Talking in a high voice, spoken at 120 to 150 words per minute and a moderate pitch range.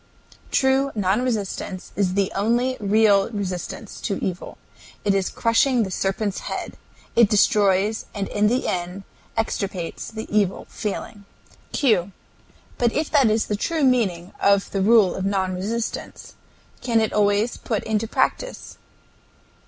Yes: high, 210 Hz; average, 140 wpm; average, 3.0 semitones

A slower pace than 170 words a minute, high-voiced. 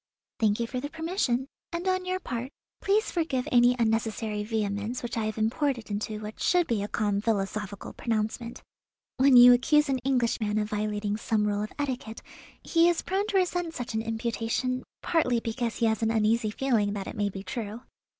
No: average, 190 wpm; high, 230 Hz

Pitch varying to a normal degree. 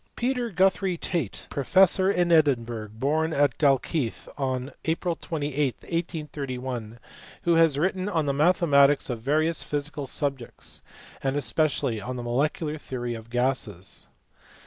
Yes: average, 4.4 semitones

